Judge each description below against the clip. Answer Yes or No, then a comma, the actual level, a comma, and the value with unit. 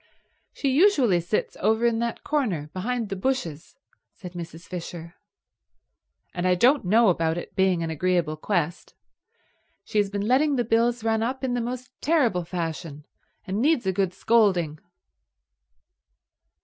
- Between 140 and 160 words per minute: Yes, average, 150 wpm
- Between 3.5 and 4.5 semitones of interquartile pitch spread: No, wide, 5.6 semitones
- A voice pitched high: Yes, high, 200 Hz